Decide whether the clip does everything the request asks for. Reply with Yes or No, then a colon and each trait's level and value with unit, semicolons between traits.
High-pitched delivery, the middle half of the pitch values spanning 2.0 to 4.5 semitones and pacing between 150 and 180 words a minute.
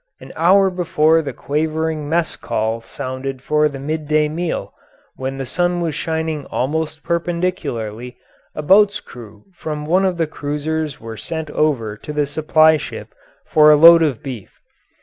No: medium, 155 Hz; average, 3.0 semitones; average, 155 wpm